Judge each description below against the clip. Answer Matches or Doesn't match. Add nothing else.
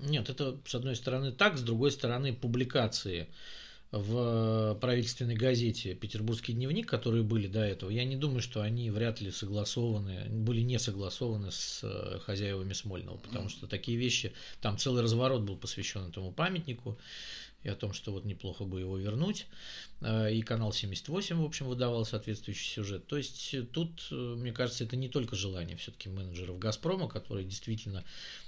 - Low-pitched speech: Matches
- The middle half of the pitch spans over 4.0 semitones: Doesn't match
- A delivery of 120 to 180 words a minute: Matches